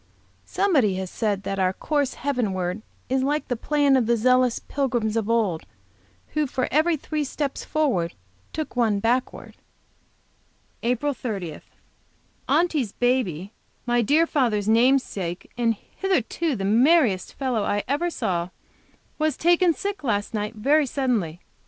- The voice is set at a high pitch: Yes, high, 245 Hz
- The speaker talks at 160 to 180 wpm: No, average, 140 wpm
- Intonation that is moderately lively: No, wide, 5.8 semitones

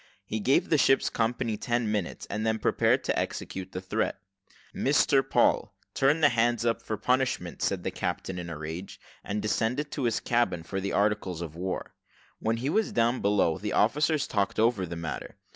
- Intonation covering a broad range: No, average, 4.2 semitones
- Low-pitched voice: Yes, low, 110 Hz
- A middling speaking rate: Yes, average, 190 wpm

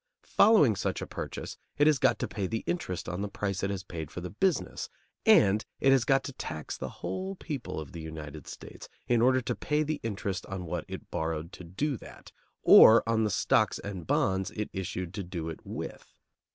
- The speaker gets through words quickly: Yes, fast, 210 wpm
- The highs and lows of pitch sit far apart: Yes, wide, 6.6 semitones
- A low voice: Yes, low, 100 Hz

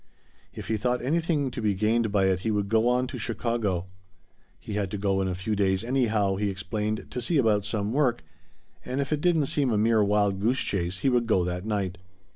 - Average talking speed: No, fast, 225 wpm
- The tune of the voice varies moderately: Yes, average, 3.9 semitones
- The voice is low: Yes, low, 110 Hz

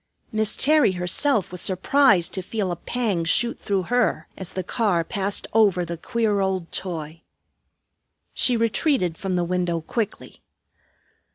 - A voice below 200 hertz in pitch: Yes, high, 190 Hz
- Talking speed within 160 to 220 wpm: No, average, 145 wpm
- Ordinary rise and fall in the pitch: Yes, average, 4.2 semitones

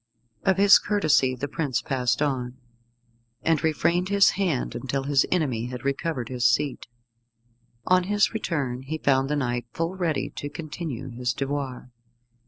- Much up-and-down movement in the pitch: No, average, 4.5 semitones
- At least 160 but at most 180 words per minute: No, average, 150 wpm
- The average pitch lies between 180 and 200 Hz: No, medium, 140 Hz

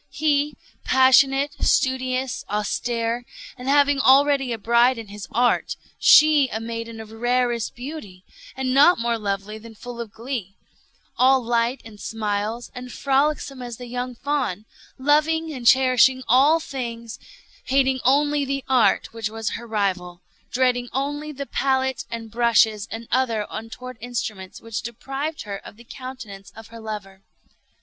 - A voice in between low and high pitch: No, high, 245 Hz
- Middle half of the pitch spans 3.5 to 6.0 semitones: No, average, 3.1 semitones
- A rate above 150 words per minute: No, average, 145 wpm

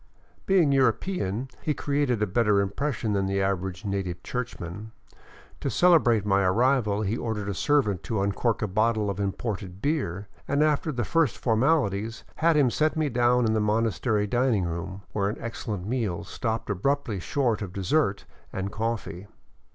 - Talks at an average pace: Yes, average, 165 wpm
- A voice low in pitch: Yes, low, 110 Hz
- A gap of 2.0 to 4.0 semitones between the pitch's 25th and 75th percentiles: No, average, 4.6 semitones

